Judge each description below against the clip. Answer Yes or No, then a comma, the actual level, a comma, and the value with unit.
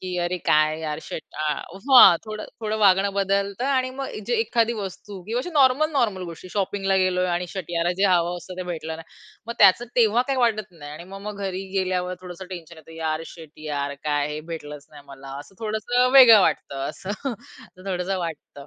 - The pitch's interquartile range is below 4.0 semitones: No, average, 4.8 semitones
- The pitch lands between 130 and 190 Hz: Yes, medium, 185 Hz